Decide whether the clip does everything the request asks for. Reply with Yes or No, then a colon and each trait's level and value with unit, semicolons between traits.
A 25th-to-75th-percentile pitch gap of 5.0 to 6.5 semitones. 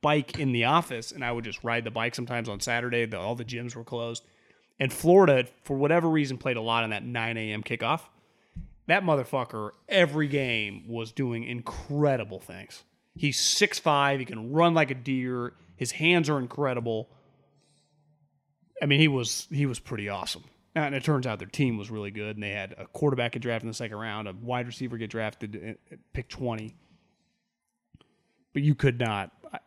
No: average, 4.1 semitones